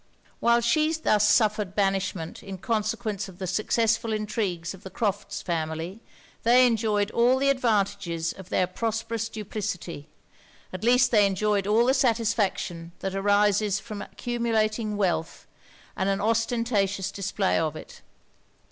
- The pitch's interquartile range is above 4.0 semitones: No, average, 3.1 semitones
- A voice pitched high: Yes, high, 210 Hz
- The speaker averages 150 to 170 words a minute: No, slow, 135 wpm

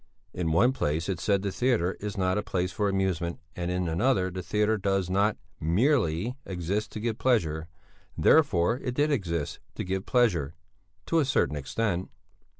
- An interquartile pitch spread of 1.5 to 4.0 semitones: No, average, 4.6 semitones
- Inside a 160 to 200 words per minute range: Yes, average, 170 wpm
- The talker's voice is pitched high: No, very low, 95 Hz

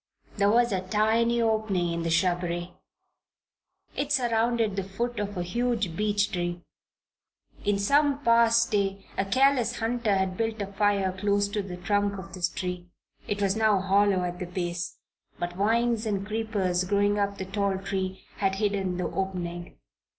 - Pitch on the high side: Yes, high, 200 Hz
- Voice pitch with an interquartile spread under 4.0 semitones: Yes, average, 3.1 semitones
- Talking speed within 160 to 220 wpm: Yes, average, 165 wpm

